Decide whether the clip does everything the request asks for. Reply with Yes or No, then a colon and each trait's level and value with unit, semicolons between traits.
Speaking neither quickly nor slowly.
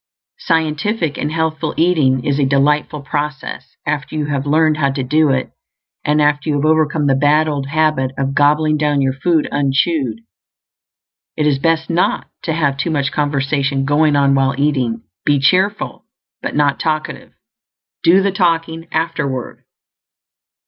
Yes: average, 155 wpm